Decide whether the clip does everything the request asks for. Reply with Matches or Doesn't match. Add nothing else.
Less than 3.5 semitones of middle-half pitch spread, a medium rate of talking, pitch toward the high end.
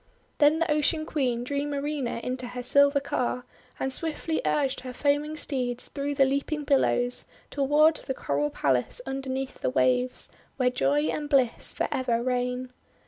Matches